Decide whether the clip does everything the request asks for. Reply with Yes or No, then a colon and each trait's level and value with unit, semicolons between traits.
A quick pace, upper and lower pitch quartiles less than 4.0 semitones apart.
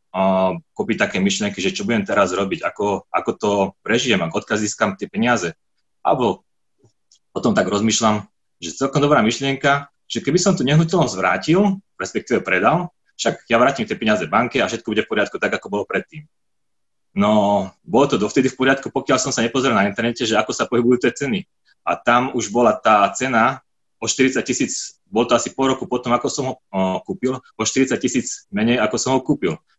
No: fast, 185 wpm; average, 4.4 semitones